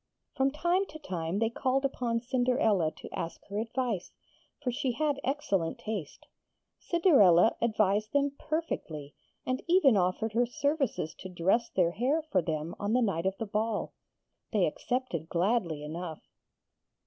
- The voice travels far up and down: Yes, wide, 6.7 semitones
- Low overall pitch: No, high, 225 Hz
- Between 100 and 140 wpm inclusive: No, average, 150 wpm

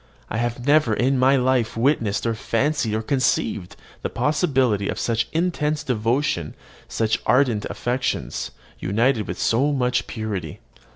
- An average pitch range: Yes, average, 3.7 semitones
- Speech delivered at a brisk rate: No, slow, 135 wpm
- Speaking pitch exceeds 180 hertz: No, low, 120 Hz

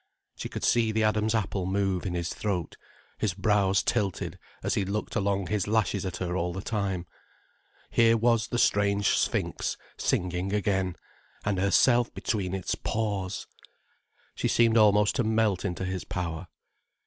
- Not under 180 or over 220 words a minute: No, average, 155 wpm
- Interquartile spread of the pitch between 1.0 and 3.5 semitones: Yes, narrow, 2.6 semitones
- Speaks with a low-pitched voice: Yes, low, 100 Hz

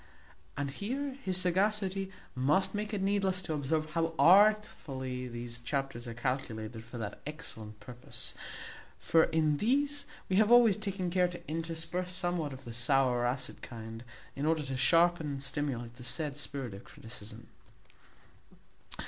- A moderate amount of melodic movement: No, wide, 6.8 semitones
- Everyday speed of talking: Yes, average, 150 wpm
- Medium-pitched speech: Yes, medium, 155 Hz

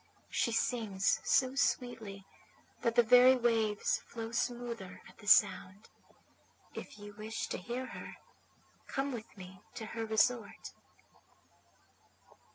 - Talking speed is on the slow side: Yes, slow, 120 wpm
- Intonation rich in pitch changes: No, average, 2.8 semitones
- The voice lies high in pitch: Yes, high, 225 Hz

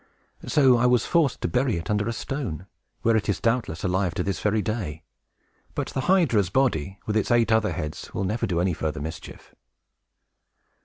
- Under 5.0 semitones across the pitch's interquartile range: No, average, 5.3 semitones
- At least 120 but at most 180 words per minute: No, average, 190 wpm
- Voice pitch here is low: Yes, low, 105 Hz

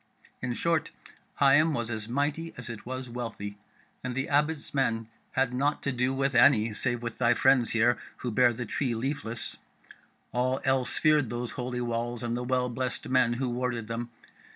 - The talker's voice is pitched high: No, low, 125 Hz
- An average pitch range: No, narrow, 2.1 semitones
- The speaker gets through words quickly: No, average, 180 wpm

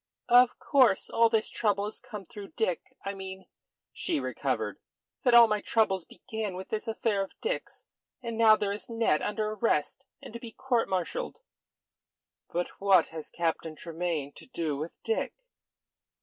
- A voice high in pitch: Yes, high, 210 Hz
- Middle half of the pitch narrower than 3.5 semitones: No, average, 4.1 semitones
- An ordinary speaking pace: Yes, average, 165 wpm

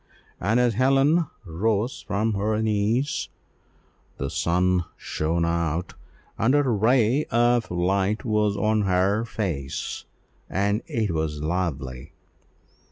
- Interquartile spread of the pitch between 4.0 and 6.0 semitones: Yes, average, 4.7 semitones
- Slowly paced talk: Yes, slow, 110 wpm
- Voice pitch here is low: Yes, low, 100 Hz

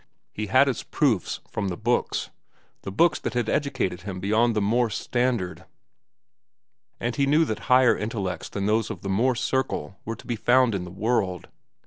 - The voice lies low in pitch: Yes, low, 110 Hz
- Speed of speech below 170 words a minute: No, average, 180 wpm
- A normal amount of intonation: Yes, average, 4.2 semitones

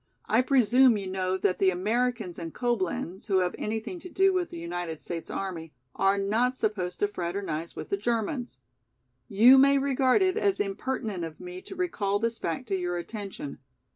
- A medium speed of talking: Yes, average, 180 wpm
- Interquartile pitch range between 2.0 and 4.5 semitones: No, wide, 5.6 semitones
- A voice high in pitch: Yes, high, 205 Hz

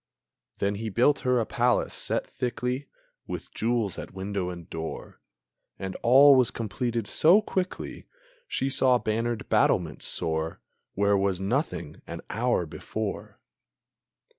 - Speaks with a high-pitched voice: No, low, 115 Hz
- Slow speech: Yes, slow, 130 wpm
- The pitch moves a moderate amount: Yes, average, 4.3 semitones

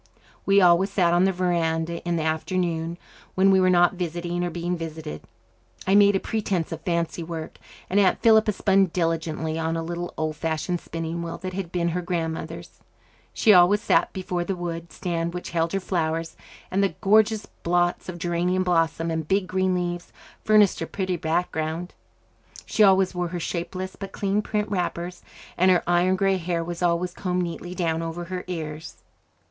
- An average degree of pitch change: No, narrow, 2.1 semitones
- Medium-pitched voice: Yes, medium, 175 Hz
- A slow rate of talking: No, average, 180 wpm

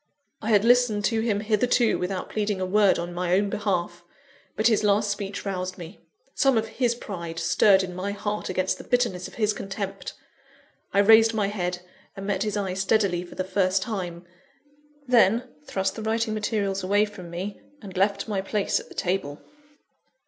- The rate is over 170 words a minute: Yes, average, 185 wpm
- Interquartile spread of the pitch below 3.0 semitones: Yes, narrow, 2.6 semitones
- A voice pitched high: Yes, high, 200 Hz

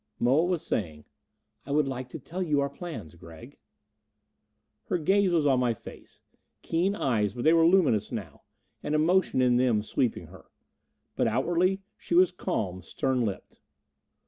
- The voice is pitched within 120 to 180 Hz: Yes, medium, 140 Hz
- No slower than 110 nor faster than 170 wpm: Yes, average, 160 wpm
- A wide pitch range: Yes, wide, 6.9 semitones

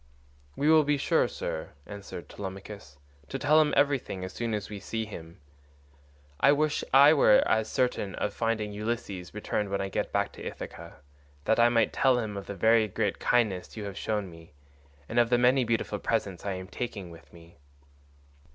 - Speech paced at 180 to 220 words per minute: Yes, average, 190 wpm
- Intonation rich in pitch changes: No, average, 3.8 semitones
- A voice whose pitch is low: Yes, low, 110 Hz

